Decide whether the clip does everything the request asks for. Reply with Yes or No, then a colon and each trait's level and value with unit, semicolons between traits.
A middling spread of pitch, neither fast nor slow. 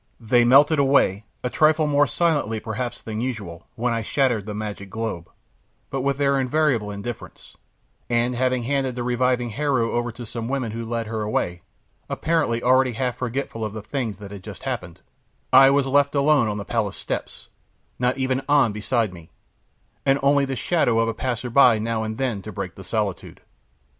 Yes: average, 3.7 semitones; average, 185 wpm